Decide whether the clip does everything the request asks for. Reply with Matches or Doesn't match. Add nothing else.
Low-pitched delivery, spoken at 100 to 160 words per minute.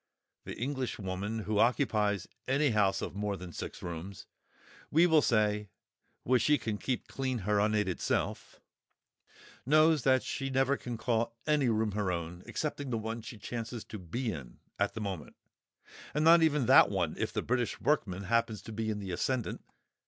Doesn't match